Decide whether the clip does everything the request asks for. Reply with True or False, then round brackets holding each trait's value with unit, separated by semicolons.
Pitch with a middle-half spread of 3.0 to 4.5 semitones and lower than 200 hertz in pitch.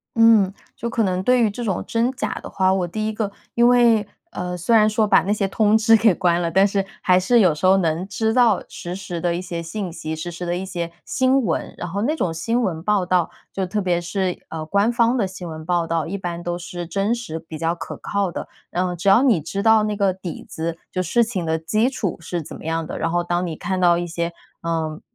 True (4.0 semitones; 185 Hz)